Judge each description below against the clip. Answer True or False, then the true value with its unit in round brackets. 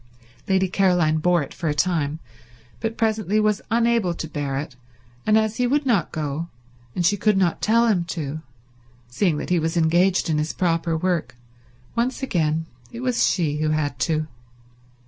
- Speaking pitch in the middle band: True (175 Hz)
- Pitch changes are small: False (5.4 semitones)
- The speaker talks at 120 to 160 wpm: False (175 wpm)